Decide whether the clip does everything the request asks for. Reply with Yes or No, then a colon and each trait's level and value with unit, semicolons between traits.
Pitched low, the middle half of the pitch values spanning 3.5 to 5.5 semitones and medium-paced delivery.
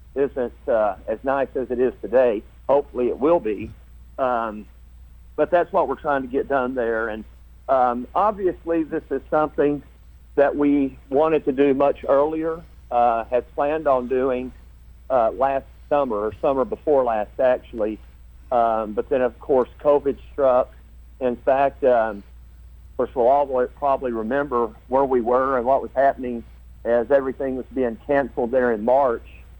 Yes: low, 125 Hz; average, 4.7 semitones; average, 160 wpm